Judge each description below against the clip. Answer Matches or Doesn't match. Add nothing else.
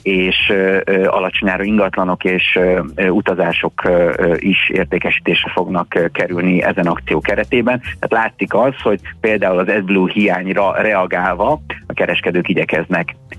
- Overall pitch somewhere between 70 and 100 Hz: Matches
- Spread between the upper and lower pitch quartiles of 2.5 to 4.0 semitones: Doesn't match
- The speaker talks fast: Doesn't match